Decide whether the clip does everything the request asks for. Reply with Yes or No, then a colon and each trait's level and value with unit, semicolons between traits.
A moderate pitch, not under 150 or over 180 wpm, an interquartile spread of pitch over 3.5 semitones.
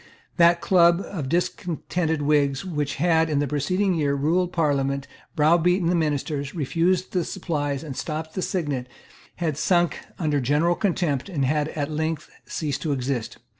No: medium, 155 Hz; average, 160 wpm; average, 3.2 semitones